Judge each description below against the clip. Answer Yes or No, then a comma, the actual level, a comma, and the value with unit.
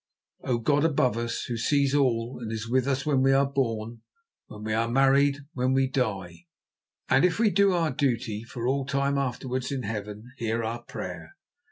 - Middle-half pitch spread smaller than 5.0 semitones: Yes, average, 3.4 semitones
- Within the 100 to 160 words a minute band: No, average, 190 wpm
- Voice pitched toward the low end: Yes, low, 125 Hz